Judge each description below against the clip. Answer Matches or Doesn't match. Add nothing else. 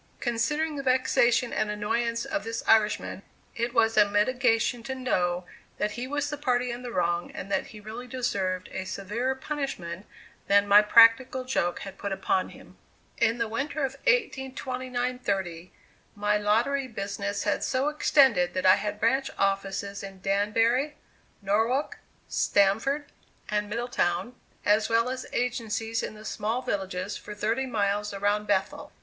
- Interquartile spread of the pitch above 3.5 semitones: Matches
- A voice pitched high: Matches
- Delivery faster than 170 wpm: Doesn't match